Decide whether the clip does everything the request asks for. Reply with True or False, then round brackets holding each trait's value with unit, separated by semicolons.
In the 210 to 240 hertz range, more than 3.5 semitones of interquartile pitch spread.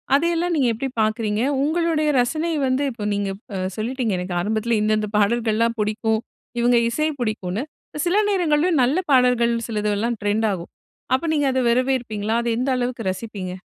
True (235 Hz; 4.1 semitones)